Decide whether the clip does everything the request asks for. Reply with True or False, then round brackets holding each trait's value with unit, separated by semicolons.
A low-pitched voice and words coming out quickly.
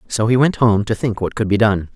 True (110 Hz; 305 wpm)